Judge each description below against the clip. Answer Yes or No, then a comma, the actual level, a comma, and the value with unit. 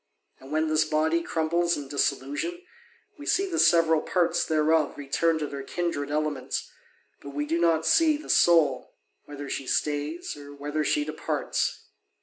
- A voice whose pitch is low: No, medium, 155 Hz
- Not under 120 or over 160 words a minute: Yes, average, 155 wpm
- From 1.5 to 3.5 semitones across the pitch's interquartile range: Yes, narrow, 2.5 semitones